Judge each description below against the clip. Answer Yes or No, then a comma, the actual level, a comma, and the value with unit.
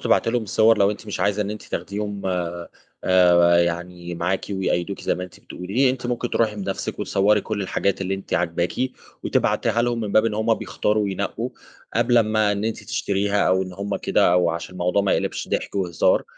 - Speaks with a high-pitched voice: No, low, 100 Hz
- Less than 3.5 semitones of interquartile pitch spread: Yes, average, 3.0 semitones